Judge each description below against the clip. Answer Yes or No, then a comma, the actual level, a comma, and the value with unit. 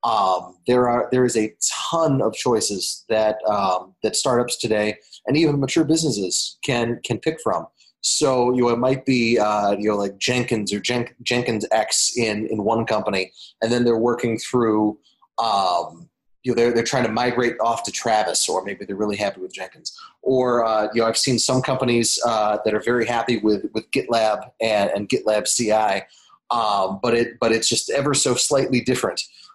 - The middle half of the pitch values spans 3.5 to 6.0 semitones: No, narrow, 2.5 semitones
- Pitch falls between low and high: No, low, 115 Hz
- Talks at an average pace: Yes, average, 190 wpm